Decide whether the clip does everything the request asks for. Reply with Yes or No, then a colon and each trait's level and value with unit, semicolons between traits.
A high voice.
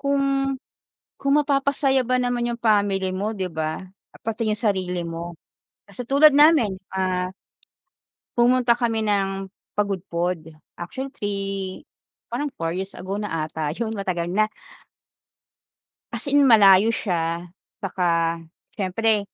Yes: high, 205 Hz